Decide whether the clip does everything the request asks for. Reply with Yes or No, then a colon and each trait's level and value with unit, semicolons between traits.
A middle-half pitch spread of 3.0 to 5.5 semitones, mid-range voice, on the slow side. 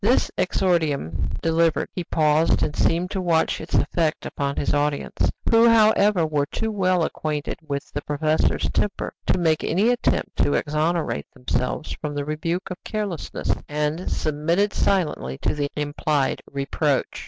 No: average, 3.7 semitones; medium, 155 Hz; average, 150 wpm